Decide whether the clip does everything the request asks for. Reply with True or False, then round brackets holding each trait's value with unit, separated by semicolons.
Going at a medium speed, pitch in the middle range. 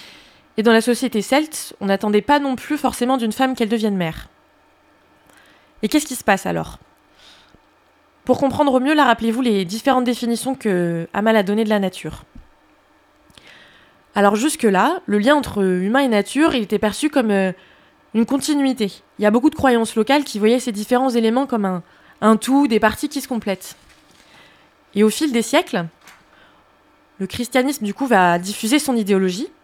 False (175 wpm; 230 Hz)